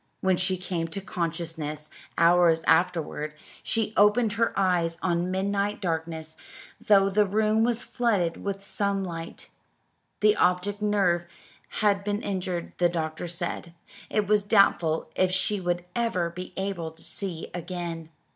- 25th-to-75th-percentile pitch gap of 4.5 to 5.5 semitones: No, average, 3.2 semitones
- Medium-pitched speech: Yes, medium, 180 Hz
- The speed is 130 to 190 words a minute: Yes, slow, 135 wpm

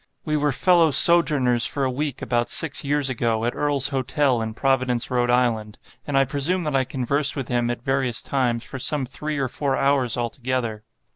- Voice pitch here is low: Yes, low, 130 Hz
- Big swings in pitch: No, average, 2.9 semitones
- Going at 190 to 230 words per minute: Yes, average, 195 wpm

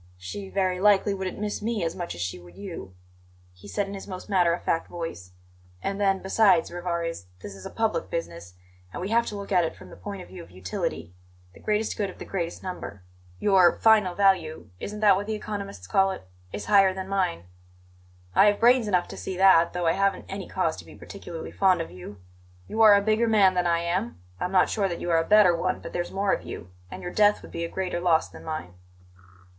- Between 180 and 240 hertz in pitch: Yes, medium, 185 Hz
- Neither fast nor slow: No, fast, 230 wpm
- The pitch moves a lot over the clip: No, average, 3.3 semitones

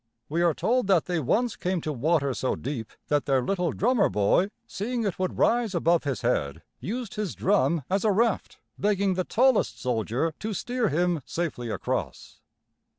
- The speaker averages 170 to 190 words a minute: Yes, average, 175 wpm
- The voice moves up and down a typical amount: No, wide, 6.5 semitones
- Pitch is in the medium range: Yes, medium, 180 Hz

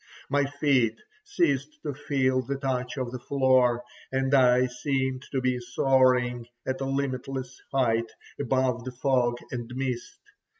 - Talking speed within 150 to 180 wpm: No, average, 140 wpm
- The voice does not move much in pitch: Yes, narrow, 1.6 semitones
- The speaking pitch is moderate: No, low, 130 Hz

